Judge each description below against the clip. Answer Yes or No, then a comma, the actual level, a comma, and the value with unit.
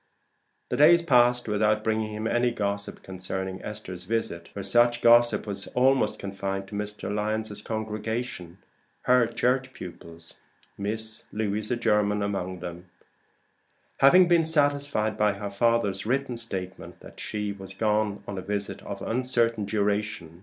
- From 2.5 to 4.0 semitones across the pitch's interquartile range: Yes, average, 3.1 semitones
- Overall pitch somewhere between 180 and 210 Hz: No, low, 105 Hz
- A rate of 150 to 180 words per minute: No, average, 140 wpm